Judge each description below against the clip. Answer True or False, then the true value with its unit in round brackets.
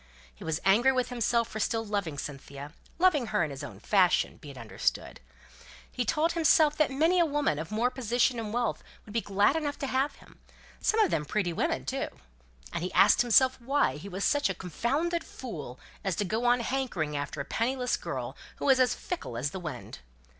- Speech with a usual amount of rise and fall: False (7.3 semitones)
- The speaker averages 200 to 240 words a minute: True (205 wpm)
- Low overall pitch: False (230 Hz)